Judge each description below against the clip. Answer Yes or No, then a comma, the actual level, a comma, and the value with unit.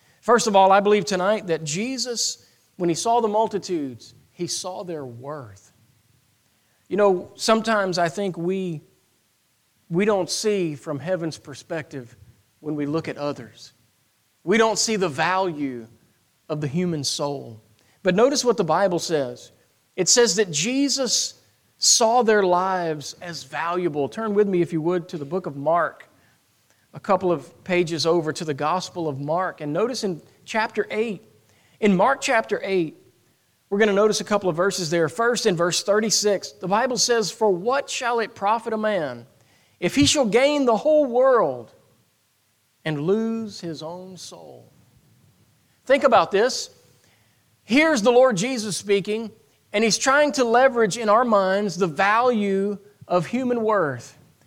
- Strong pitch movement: Yes, wide, 6.5 semitones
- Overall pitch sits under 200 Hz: Yes, medium, 185 Hz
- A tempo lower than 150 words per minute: No, average, 160 wpm